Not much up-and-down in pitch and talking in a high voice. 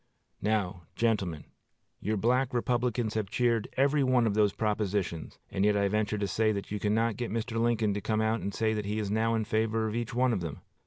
No: narrow, 2.1 semitones; low, 110 Hz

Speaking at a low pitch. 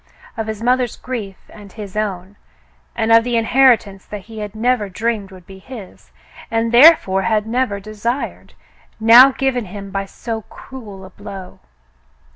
No: high, 220 Hz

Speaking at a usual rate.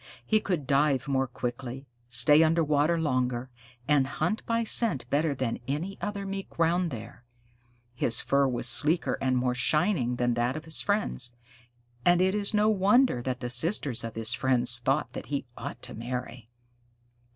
Yes: average, 170 wpm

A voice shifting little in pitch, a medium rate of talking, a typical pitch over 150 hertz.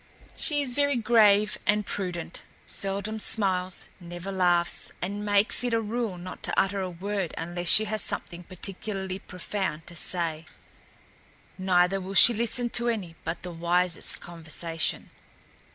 No: average, 3.3 semitones; average, 145 wpm; high, 190 Hz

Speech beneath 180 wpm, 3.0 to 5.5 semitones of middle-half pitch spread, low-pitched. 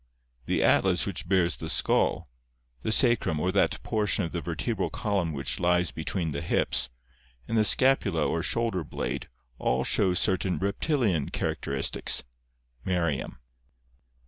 Yes: average, 140 wpm; average, 4.4 semitones; very low, 90 Hz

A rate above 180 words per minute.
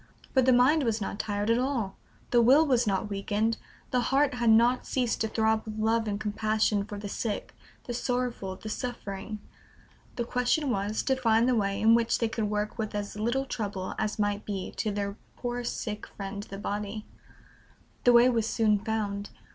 Yes: average, 190 wpm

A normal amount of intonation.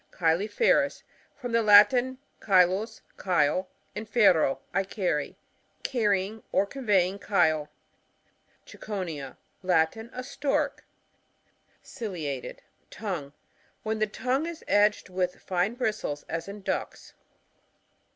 Yes: average, 3.9 semitones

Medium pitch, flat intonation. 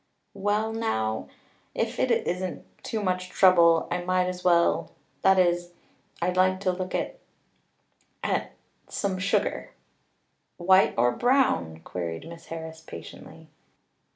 Yes: medium, 180 Hz; narrow, 2.2 semitones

